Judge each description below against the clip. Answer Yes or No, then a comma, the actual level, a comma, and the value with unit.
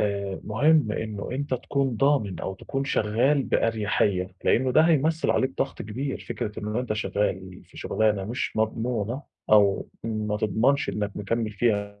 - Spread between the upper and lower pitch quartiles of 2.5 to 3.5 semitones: No, average, 4.2 semitones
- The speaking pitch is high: No, low, 110 Hz